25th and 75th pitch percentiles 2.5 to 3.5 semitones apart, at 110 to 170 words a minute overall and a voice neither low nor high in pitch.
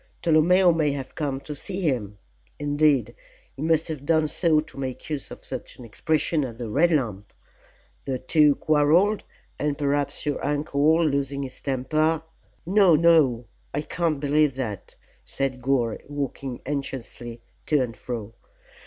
Yes: average, 3.2 semitones; average, 155 wpm; medium, 145 Hz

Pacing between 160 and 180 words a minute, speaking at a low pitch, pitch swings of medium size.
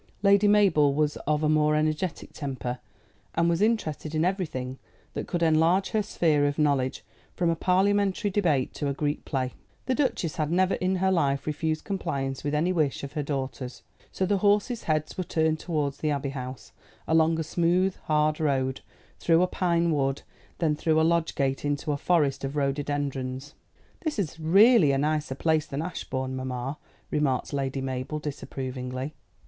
No: average, 175 wpm; medium, 155 Hz; average, 3.8 semitones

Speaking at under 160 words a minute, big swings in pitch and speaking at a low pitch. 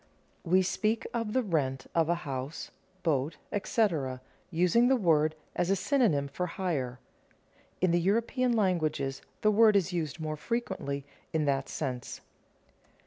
No: average, 145 wpm; wide, 6.7 semitones; medium, 170 Hz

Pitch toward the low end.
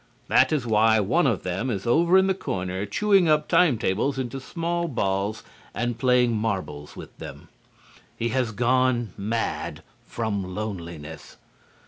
Yes: low, 115 Hz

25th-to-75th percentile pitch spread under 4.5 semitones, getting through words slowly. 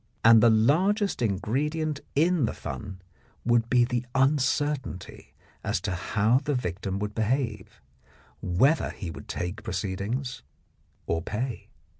No: average, 5.3 semitones; slow, 125 wpm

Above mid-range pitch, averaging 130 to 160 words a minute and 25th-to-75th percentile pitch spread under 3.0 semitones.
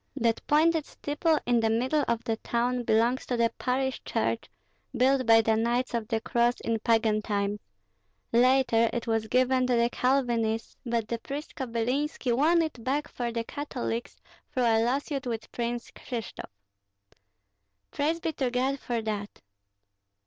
Yes: high, 240 Hz; average, 155 wpm; narrow, 2.6 semitones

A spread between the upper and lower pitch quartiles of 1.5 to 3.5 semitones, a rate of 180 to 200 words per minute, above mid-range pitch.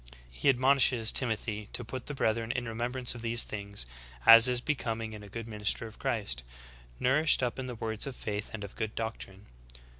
No: narrow, 2.6 semitones; average, 190 wpm; low, 115 Hz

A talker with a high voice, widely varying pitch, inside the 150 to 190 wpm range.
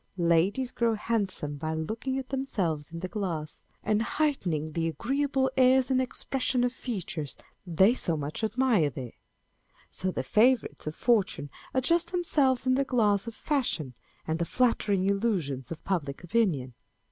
Yes: high, 210 Hz; wide, 7.9 semitones; average, 155 wpm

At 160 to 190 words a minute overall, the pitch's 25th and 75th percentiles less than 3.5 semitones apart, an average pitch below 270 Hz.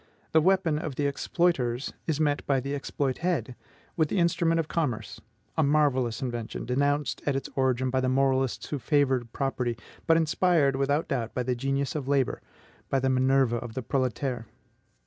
Yes: average, 170 wpm; average, 2.8 semitones; low, 135 Hz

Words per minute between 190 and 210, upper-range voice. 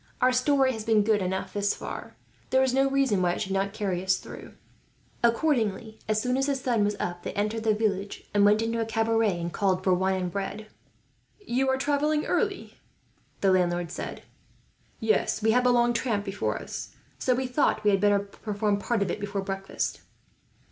Yes: average, 200 wpm; high, 215 Hz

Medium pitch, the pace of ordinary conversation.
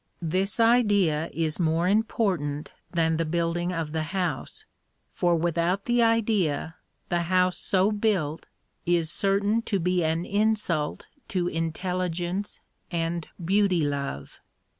No: medium, 175 Hz; slow, 120 wpm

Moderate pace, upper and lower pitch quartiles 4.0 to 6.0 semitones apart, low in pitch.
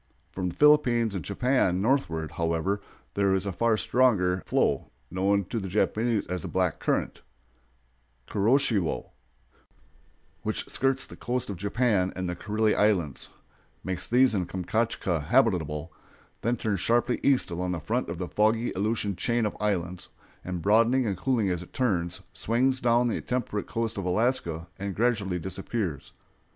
Yes: average, 155 wpm; average, 4.5 semitones; low, 100 Hz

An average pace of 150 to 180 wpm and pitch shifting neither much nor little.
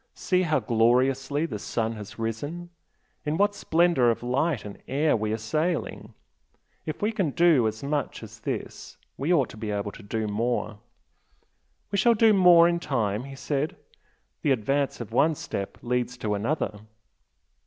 No: average, 165 wpm; wide, 6.4 semitones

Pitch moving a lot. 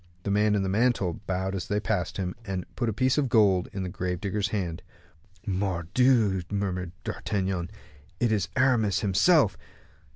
No: average, 2.9 semitones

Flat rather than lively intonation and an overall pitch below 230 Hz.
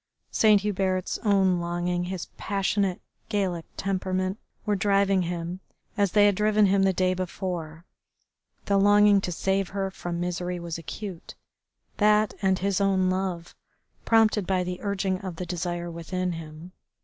Yes: narrow, 2.1 semitones; medium, 185 Hz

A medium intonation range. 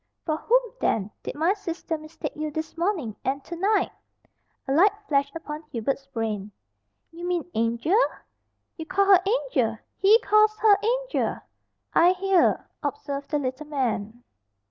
No: wide, 6.3 semitones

